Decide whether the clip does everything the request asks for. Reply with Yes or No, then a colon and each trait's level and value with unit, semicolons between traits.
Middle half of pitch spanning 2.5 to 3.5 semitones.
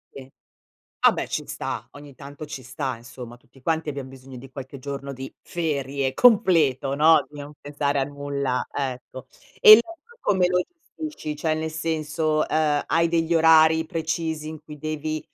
Yes: average, 2.8 semitones